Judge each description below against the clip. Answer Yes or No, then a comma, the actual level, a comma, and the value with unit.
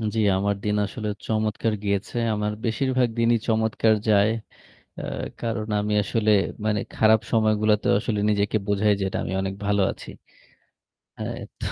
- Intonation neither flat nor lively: No, narrow, 1.4 semitones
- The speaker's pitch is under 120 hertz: Yes, low, 110 Hz